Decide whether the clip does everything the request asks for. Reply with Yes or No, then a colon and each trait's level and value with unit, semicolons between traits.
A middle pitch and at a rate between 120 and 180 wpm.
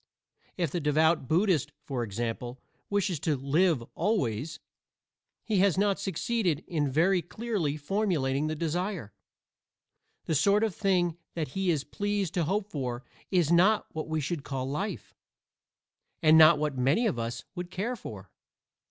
Yes: medium, 165 Hz; average, 150 wpm